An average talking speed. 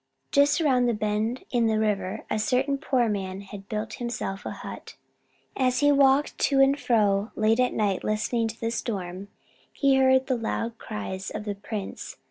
Yes: average, 180 wpm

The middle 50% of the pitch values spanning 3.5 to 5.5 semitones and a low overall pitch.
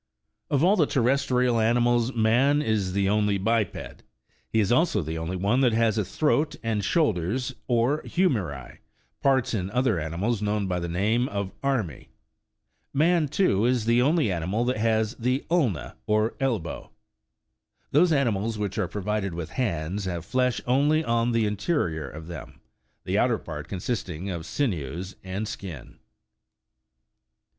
Yes: average, 5.2 semitones; low, 110 Hz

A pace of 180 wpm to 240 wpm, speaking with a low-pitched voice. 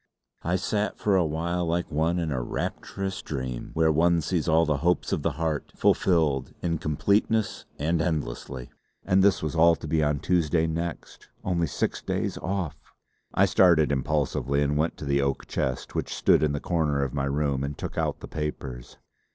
Yes: average, 185 wpm; very low, 80 Hz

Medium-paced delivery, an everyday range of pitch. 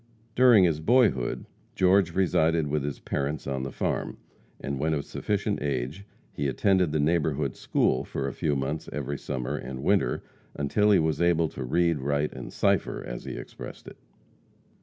Yes: average, 170 wpm; average, 4.2 semitones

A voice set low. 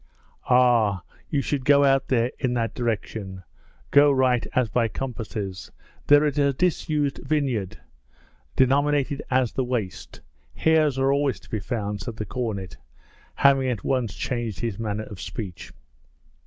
Yes: low, 125 Hz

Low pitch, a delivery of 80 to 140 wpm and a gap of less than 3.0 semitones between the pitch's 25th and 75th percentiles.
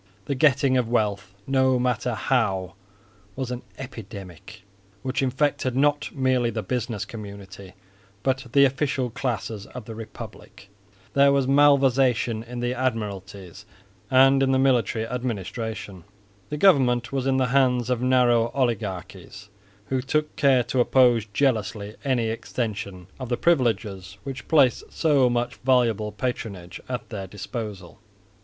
No: low, 120 Hz; slow, 135 wpm; average, 3.7 semitones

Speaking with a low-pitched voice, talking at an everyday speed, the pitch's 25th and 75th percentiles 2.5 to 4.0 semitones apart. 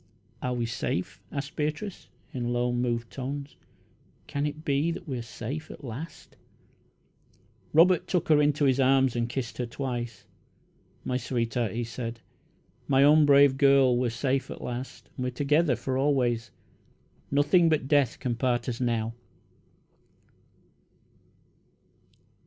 Yes: low, 130 Hz; average, 145 wpm; average, 3.2 semitones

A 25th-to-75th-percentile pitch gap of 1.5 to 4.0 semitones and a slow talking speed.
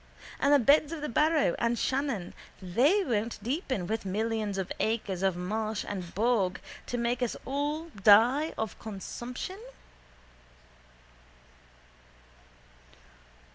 No: wide, 5.6 semitones; slow, 115 wpm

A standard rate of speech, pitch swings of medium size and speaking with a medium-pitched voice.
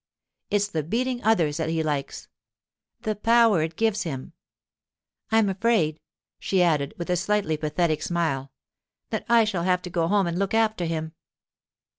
Yes: average, 155 wpm; average, 4.9 semitones; medium, 180 Hz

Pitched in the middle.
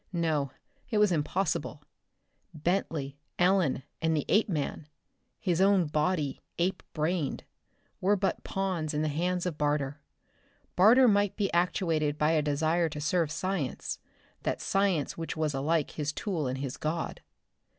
Yes: medium, 165 Hz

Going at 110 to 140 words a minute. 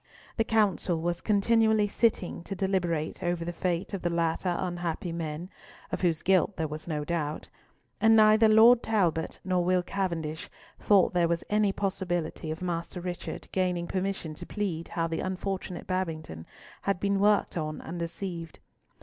No: average, 160 wpm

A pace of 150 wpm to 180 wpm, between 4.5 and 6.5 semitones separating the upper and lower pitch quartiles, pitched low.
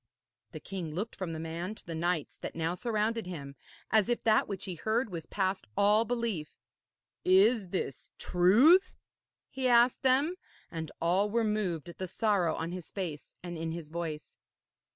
No: average, 170 wpm; average, 4.8 semitones; medium, 185 Hz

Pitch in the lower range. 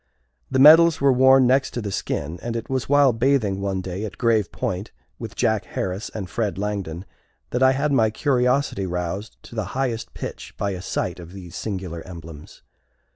Yes: low, 110 Hz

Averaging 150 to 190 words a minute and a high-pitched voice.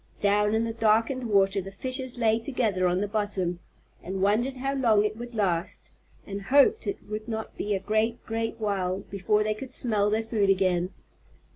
Yes: average, 185 wpm; high, 215 Hz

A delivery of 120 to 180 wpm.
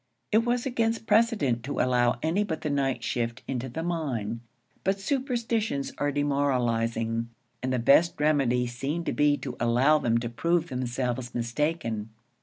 Yes: average, 155 wpm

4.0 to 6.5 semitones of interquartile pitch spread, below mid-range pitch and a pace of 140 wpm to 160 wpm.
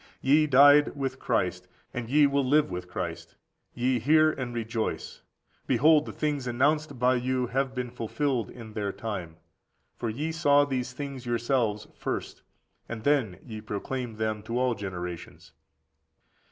Yes: average, 4.3 semitones; low, 125 Hz; average, 150 wpm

